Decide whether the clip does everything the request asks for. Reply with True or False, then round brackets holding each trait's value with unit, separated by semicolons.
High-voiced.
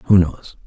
False (90 Hz)